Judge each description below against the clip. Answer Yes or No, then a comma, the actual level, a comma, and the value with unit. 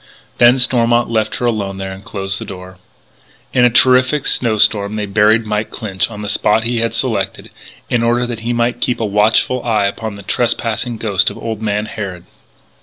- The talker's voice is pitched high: No, low, 110 Hz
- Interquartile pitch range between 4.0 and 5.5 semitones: No, average, 2.7 semitones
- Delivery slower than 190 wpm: No, average, 195 wpm